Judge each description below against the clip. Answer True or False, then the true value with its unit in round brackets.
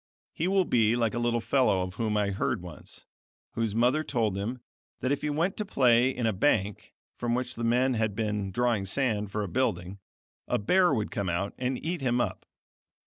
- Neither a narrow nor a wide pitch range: True (3.9 semitones)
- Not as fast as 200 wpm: False (205 wpm)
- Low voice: True (115 Hz)